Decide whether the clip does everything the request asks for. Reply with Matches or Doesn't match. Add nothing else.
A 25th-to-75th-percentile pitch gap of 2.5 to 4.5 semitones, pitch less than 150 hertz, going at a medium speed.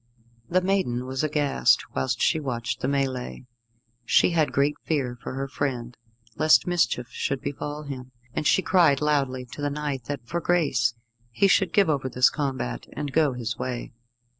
Matches